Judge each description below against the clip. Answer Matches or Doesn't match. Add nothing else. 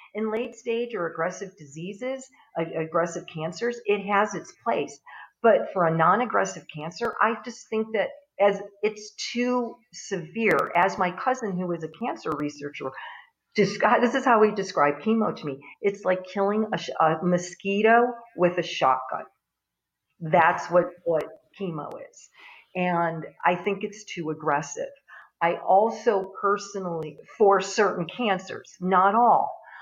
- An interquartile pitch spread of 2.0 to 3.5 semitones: Doesn't match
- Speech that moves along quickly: Doesn't match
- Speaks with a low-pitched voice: Doesn't match